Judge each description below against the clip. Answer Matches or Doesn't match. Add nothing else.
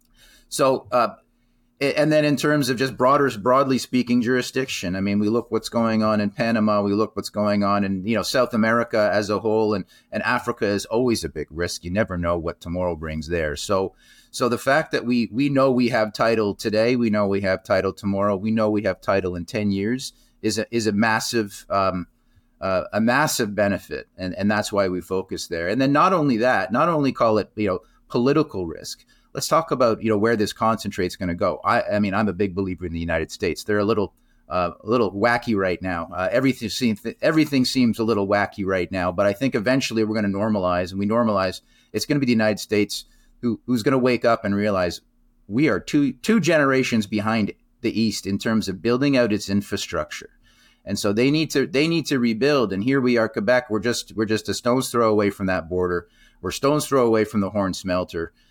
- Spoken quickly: Matches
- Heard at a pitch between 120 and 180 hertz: Doesn't match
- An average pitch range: Matches